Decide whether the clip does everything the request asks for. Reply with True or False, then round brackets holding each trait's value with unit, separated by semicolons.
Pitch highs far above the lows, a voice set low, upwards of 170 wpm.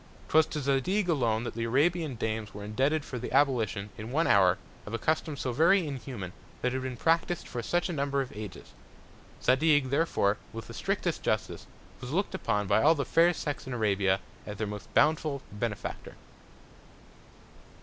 True (6.1 semitones; 130 Hz; 180 wpm)